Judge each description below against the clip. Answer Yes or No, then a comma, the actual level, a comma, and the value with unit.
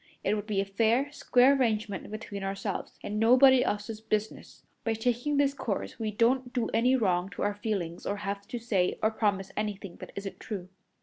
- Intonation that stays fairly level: No, average, 3.2 semitones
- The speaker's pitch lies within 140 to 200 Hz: No, high, 215 Hz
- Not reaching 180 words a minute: No, average, 190 wpm